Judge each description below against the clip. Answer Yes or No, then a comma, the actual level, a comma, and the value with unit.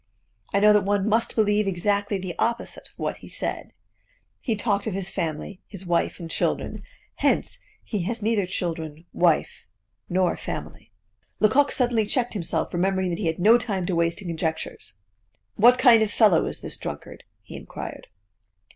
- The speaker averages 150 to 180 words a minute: Yes, average, 170 wpm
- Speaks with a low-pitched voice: No, high, 200 Hz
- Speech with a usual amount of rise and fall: Yes, average, 3.9 semitones